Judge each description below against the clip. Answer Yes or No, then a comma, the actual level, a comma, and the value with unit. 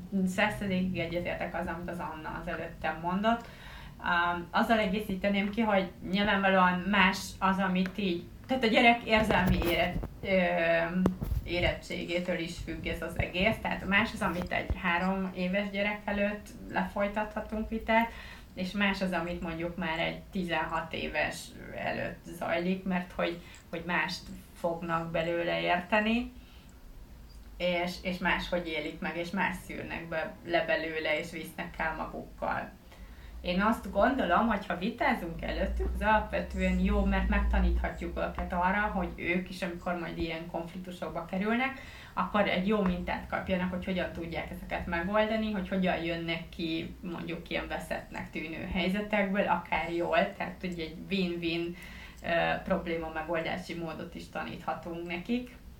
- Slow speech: No, average, 135 wpm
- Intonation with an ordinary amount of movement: Yes, average, 3.2 semitones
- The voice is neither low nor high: Yes, medium, 180 Hz